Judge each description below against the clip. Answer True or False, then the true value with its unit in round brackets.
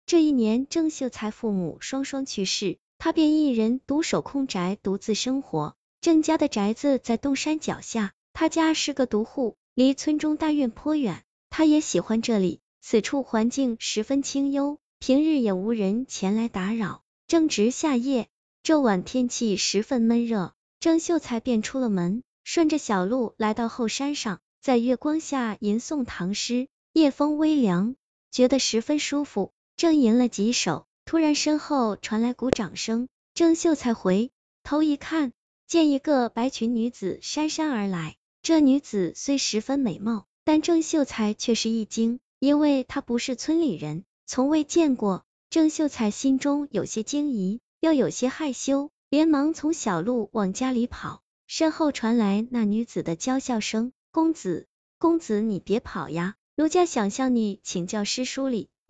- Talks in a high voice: True (255 Hz)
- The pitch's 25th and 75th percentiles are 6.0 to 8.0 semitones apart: False (5.3 semitones)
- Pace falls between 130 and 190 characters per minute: False (230 characters per minute)